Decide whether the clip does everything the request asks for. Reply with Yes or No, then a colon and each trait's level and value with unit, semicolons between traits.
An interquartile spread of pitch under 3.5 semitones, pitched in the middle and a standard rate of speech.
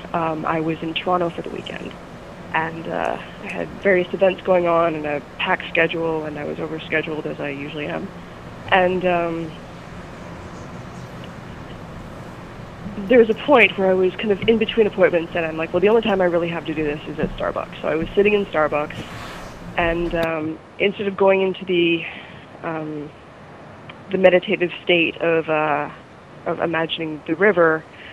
Yes: average, 3.1 semitones; medium, 165 Hz; average, 175 wpm